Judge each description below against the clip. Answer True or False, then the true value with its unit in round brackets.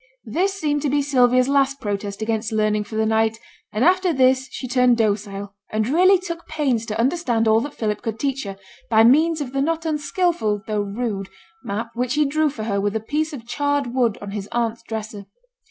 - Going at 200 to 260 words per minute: True (205 wpm)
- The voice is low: False (240 Hz)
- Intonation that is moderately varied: True (5.0 semitones)